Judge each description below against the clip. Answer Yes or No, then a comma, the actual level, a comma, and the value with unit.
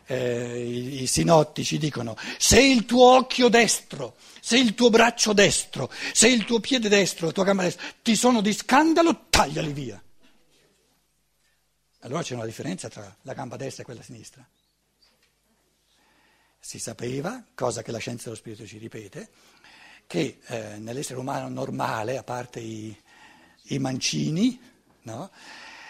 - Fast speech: No, average, 140 wpm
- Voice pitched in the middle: Yes, medium, 155 Hz